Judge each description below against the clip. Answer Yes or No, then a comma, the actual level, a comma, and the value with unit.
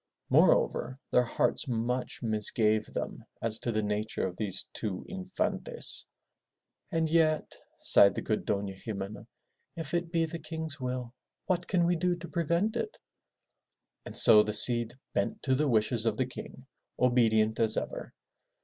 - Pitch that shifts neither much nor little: No, wide, 7.1 semitones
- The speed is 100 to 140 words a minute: No, average, 155 wpm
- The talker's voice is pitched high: No, low, 125 Hz